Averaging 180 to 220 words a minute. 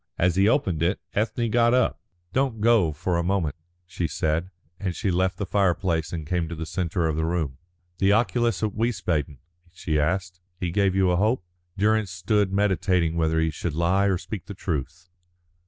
Yes: average, 190 wpm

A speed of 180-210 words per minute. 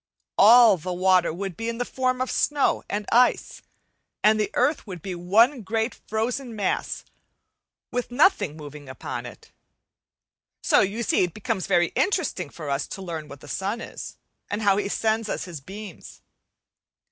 No: average, 165 wpm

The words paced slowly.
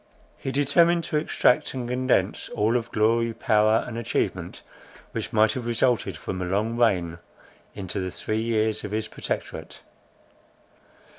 No: average, 145 wpm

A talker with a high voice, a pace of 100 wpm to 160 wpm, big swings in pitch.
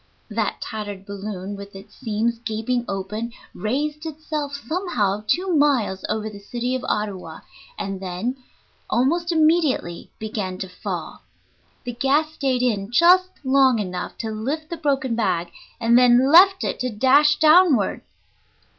Yes: high, 240 Hz; average, 140 wpm; wide, 6.0 semitones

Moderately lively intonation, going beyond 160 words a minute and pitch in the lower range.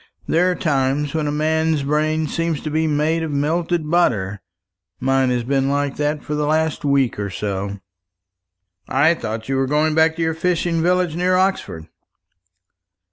No: average, 3.2 semitones; average, 170 wpm; medium, 150 Hz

